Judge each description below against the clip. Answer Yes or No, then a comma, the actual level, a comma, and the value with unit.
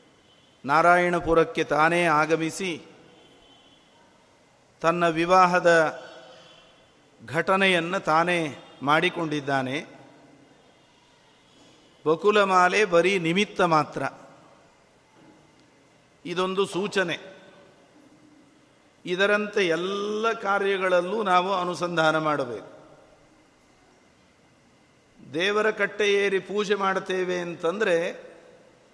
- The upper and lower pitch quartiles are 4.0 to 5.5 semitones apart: No, average, 3.3 semitones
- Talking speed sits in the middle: No, slow, 55 wpm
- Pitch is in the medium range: Yes, medium, 175 Hz